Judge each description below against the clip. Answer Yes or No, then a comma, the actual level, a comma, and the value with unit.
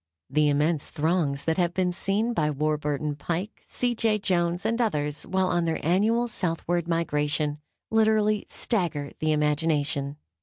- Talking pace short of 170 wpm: Yes, average, 145 wpm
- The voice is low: No, medium, 165 Hz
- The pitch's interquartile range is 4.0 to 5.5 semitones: Yes, average, 4.6 semitones